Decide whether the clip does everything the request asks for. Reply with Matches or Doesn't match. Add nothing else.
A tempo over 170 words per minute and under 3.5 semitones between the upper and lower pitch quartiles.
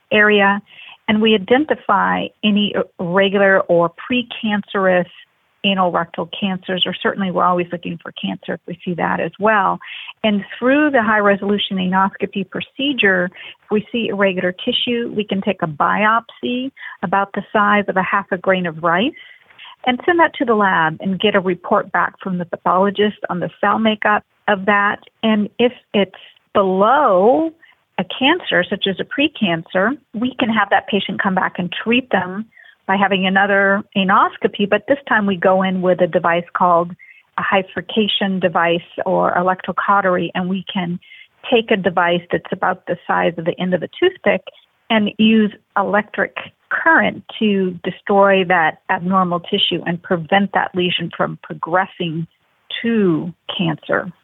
Doesn't match